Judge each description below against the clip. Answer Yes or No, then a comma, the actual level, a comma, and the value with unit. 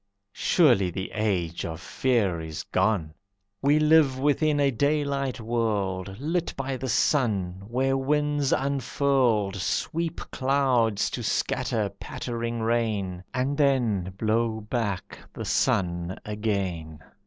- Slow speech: Yes, slow, 115 wpm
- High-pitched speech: No, low, 115 Hz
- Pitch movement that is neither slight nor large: No, wide, 5.7 semitones